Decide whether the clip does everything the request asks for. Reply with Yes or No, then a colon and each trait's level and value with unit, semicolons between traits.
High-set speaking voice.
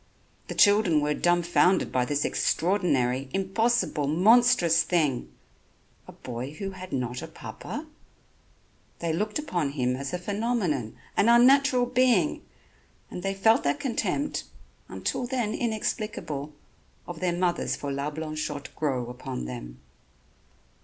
No: medium, 175 Hz